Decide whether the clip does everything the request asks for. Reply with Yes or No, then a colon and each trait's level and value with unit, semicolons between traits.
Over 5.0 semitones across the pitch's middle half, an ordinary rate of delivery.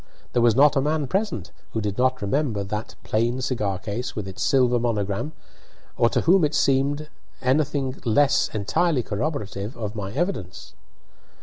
Yes: wide, 5.5 semitones; average, 160 wpm